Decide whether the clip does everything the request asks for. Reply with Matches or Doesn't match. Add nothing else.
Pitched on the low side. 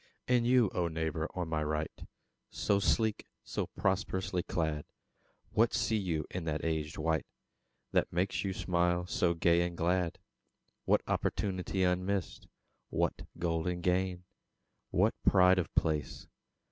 Matches